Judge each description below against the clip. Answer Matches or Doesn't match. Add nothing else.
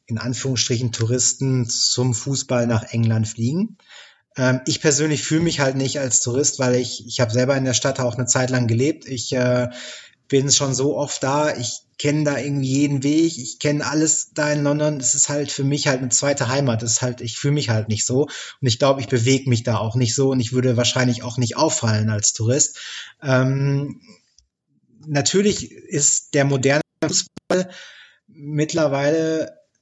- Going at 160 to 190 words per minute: Matches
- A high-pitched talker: Doesn't match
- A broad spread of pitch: Doesn't match